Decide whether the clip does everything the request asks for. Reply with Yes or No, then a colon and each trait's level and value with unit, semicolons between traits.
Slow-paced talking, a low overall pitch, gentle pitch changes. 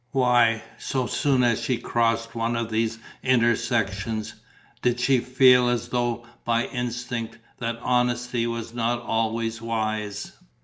Yes: slow, 130 wpm; low, 120 Hz; narrow, 1.3 semitones